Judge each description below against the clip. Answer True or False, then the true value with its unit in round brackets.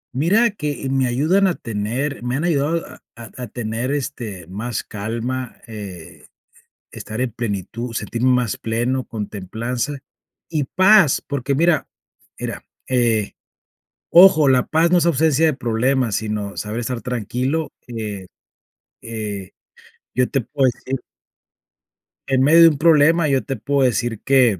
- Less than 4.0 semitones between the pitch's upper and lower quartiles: False (4.4 semitones)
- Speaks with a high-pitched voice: False (125 Hz)